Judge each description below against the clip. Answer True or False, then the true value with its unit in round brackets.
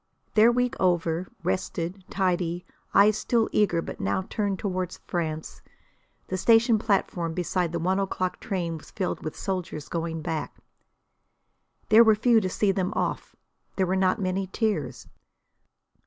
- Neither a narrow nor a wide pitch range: True (3.4 semitones)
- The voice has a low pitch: False (185 Hz)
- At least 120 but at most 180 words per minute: True (145 wpm)